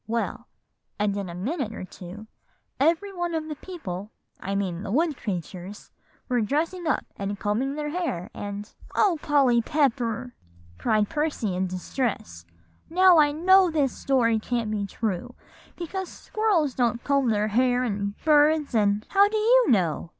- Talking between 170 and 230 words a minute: No, average, 155 wpm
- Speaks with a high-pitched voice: Yes, high, 245 Hz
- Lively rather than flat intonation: Yes, wide, 7.4 semitones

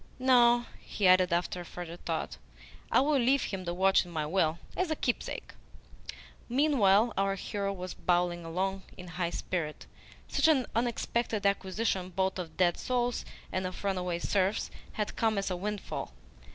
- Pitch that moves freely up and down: No, average, 4.4 semitones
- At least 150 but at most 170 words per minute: Yes, average, 160 wpm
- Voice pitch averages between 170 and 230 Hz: Yes, high, 190 Hz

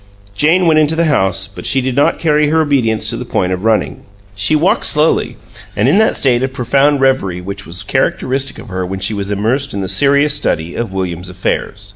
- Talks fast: Yes, fast, 215 wpm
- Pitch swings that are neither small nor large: No, wide, 6.9 semitones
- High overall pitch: No, low, 120 Hz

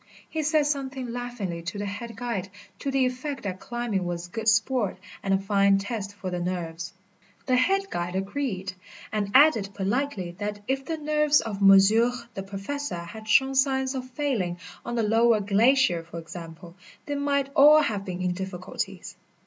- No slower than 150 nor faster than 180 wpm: Yes, average, 175 wpm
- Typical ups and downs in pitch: No, wide, 5.9 semitones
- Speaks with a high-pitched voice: Yes, high, 215 Hz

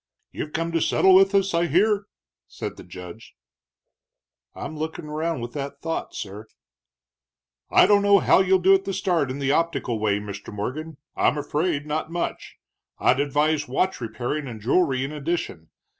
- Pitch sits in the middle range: Yes, medium, 150 Hz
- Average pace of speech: Yes, average, 170 wpm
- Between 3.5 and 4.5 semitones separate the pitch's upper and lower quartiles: No, average, 5.3 semitones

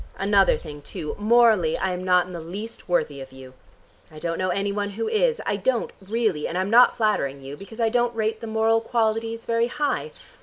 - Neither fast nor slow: No, fast, 215 wpm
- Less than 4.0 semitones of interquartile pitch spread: No, average, 4.4 semitones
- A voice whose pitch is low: No, high, 205 Hz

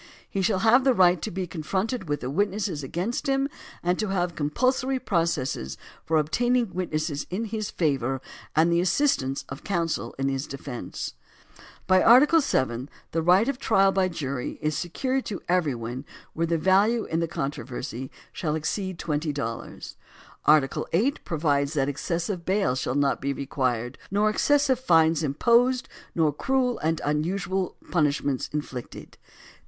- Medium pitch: Yes, medium, 170 Hz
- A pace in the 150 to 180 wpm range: Yes, average, 160 wpm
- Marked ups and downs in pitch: Yes, wide, 6.0 semitones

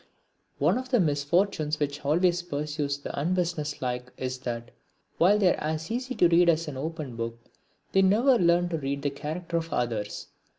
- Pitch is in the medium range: Yes, medium, 155 Hz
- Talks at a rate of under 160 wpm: No, average, 175 wpm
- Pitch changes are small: No, average, 3.9 semitones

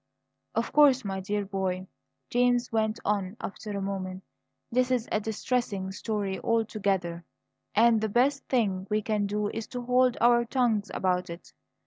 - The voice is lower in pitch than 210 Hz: No, high, 215 Hz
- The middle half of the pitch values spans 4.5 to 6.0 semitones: No, average, 3.7 semitones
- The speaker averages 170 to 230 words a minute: No, average, 155 wpm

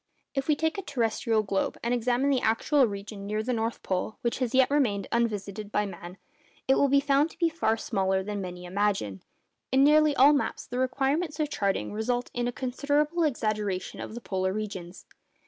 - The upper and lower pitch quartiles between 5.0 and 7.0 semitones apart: Yes, wide, 5.5 semitones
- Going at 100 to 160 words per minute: No, average, 200 wpm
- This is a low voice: No, high, 235 Hz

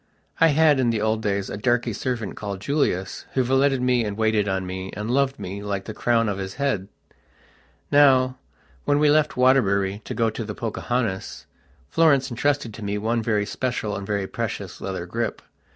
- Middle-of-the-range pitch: No, low, 115 Hz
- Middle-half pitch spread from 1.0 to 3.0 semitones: No, average, 4.3 semitones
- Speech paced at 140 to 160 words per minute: No, average, 185 wpm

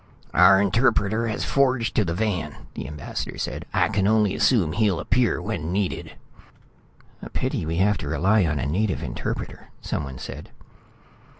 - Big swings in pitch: No, average, 4.8 semitones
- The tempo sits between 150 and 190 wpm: Yes, average, 160 wpm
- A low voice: Yes, low, 100 Hz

